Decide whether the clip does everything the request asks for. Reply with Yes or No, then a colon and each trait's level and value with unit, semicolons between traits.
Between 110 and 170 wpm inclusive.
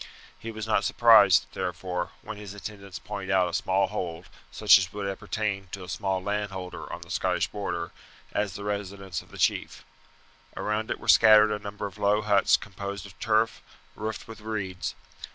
No: average, 180 wpm